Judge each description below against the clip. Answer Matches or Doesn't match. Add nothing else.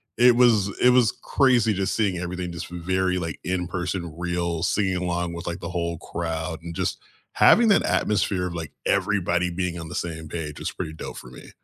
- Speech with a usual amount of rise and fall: Doesn't match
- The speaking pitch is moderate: Doesn't match